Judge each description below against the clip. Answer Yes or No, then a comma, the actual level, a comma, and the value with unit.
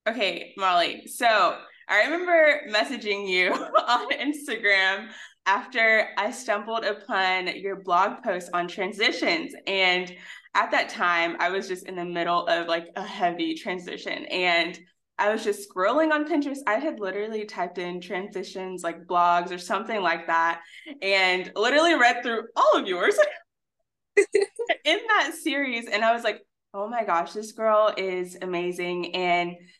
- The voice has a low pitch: No, high, 200 Hz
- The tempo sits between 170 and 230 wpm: No, average, 150 wpm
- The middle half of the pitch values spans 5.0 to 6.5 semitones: Yes, average, 5.3 semitones